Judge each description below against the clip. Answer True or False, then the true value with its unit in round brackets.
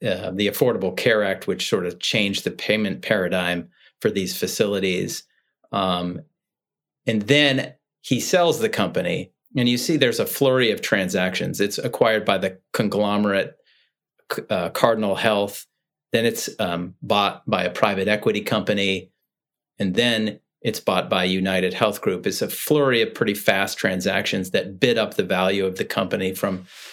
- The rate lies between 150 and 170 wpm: True (160 wpm)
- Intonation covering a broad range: False (3.1 semitones)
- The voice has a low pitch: True (100 Hz)